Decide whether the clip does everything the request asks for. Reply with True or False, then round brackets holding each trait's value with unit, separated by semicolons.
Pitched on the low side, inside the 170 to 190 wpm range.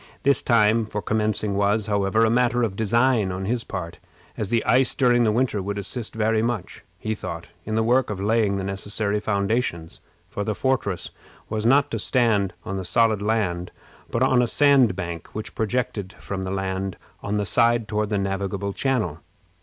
True (105 Hz; 185 wpm)